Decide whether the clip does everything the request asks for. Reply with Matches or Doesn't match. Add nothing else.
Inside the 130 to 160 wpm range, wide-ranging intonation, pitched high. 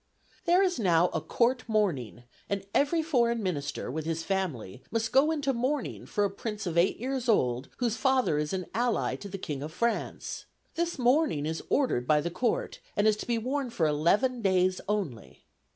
Doesn't match